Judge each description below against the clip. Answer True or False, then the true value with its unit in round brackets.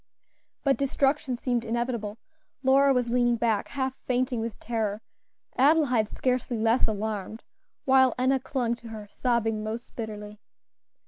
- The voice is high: True (240 Hz)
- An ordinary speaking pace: False (130 wpm)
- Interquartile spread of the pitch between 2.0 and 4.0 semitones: True (2.9 semitones)